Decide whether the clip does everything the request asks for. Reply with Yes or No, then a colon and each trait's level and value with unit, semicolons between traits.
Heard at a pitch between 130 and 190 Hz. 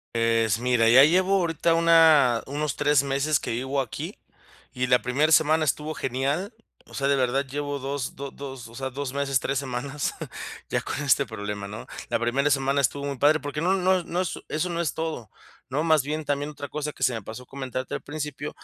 Yes: medium, 140 Hz